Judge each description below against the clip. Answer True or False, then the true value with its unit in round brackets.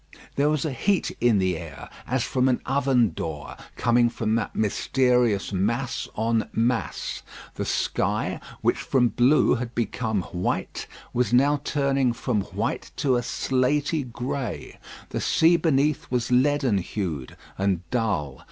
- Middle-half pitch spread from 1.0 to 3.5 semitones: False (4.1 semitones)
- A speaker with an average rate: True (145 wpm)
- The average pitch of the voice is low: True (120 Hz)